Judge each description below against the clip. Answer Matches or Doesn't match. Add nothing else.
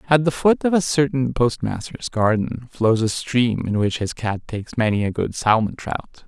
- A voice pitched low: Matches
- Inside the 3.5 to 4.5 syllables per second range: Doesn't match